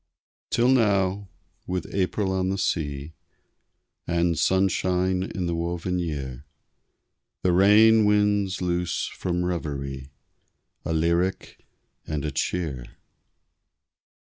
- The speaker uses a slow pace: Yes, slow, 100 wpm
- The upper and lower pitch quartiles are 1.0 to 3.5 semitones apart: Yes, average, 2.8 semitones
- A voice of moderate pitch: No, very low, 90 Hz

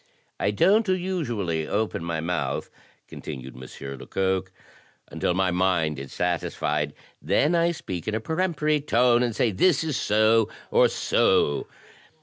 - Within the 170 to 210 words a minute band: No, slow, 135 wpm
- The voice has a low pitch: Yes, low, 100 Hz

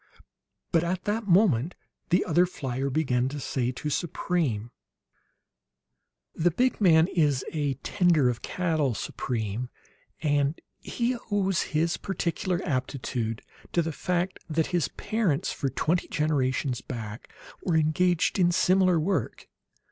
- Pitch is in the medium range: Yes, medium, 160 Hz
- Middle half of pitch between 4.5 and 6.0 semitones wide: Yes, average, 5.1 semitones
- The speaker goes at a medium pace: No, slow, 125 wpm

